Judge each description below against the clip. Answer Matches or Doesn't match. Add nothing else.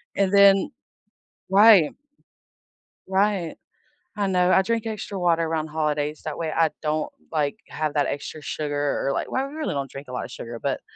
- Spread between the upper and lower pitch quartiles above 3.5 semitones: Matches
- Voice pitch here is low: Doesn't match